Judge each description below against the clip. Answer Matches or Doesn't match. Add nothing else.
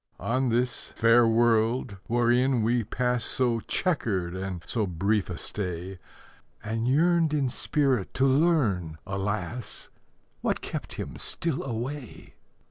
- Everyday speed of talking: Doesn't match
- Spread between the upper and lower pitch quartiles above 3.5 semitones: Matches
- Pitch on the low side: Matches